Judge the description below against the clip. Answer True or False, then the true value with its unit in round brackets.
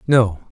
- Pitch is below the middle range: True (110 Hz)